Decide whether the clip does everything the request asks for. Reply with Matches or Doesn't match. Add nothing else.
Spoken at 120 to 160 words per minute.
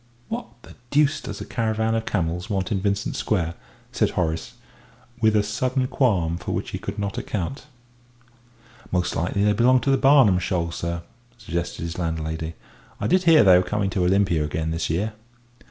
Doesn't match